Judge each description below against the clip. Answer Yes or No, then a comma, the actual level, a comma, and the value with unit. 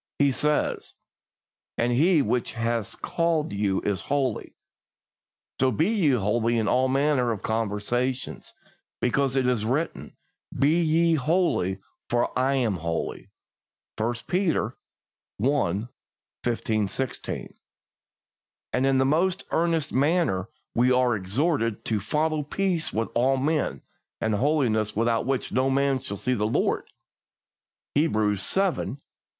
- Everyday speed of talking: No, slow, 130 wpm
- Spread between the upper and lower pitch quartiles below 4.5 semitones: No, average, 5.1 semitones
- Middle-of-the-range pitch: No, low, 130 Hz